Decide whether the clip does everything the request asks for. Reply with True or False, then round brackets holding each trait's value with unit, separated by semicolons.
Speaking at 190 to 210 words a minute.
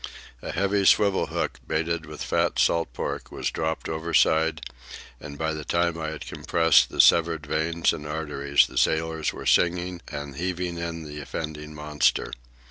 False (160 wpm)